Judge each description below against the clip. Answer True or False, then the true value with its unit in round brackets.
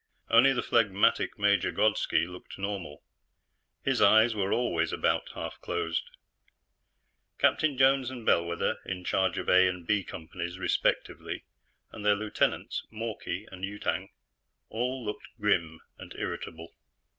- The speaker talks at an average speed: False (130 wpm)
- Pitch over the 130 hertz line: False (100 Hz)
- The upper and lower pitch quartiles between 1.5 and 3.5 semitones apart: False (4.0 semitones)